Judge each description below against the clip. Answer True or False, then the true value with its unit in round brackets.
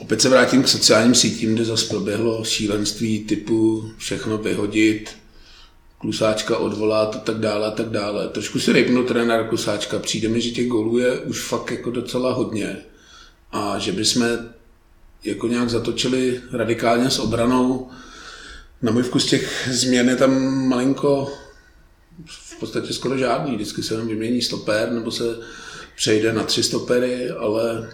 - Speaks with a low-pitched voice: True (115 Hz)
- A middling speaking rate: True (150 wpm)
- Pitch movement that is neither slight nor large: False (2.2 semitones)